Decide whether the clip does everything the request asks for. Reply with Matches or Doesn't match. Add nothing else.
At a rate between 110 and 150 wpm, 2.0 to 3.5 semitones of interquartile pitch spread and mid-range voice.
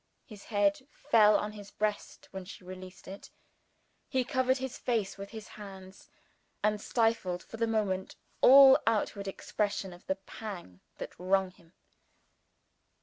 Doesn't match